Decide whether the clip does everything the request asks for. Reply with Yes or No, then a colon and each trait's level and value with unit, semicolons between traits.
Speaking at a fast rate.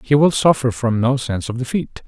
Yes: fast, 230 wpm